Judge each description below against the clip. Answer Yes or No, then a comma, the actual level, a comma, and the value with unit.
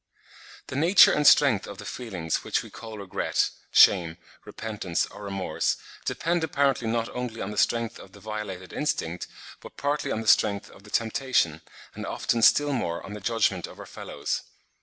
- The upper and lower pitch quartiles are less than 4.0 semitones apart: No, average, 4.4 semitones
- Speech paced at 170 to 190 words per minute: Yes, average, 180 wpm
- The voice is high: No, low, 110 Hz